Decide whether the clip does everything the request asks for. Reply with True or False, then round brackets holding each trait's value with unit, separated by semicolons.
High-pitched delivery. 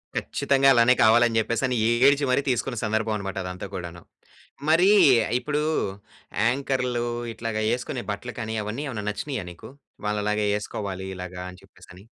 False (115 Hz)